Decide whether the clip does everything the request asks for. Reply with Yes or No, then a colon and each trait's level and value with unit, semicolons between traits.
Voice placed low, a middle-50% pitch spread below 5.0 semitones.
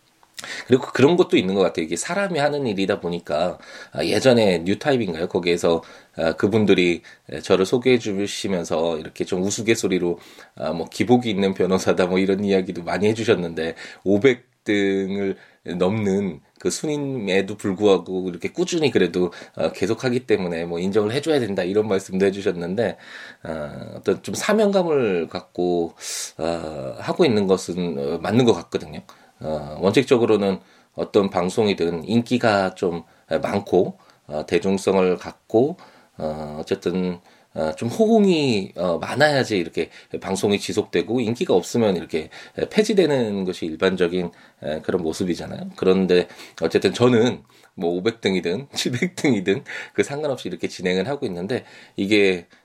Yes: very low, 95 Hz; average, 4.5 semitones